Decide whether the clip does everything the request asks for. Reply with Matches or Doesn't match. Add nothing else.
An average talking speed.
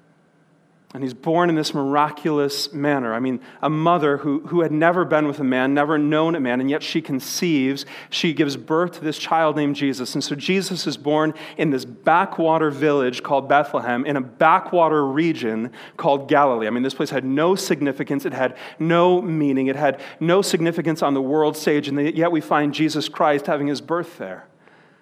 Matches